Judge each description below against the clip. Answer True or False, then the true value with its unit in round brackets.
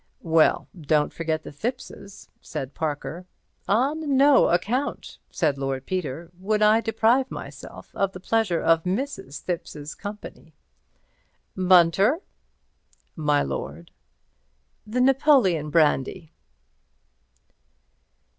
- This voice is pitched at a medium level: True (180 Hz)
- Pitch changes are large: True (6.6 semitones)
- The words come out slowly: True (100 wpm)